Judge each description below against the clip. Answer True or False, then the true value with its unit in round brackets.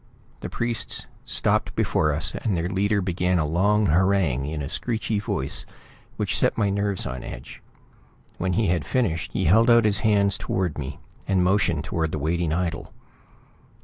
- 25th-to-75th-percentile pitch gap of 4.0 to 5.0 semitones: True (4.3 semitones)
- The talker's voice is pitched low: True (90 Hz)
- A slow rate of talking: False (170 wpm)